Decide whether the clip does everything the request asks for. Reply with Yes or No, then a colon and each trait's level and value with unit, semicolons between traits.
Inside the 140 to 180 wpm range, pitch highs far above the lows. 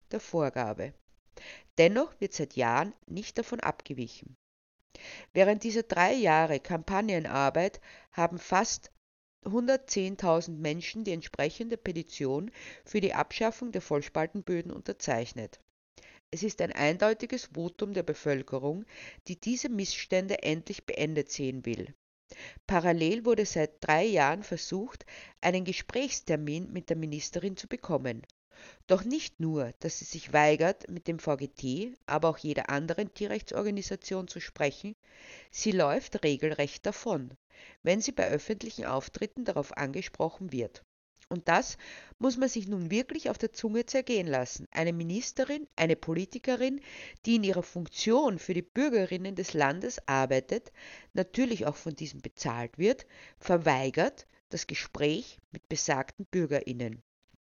No: slow, 125 wpm; wide, 6.2 semitones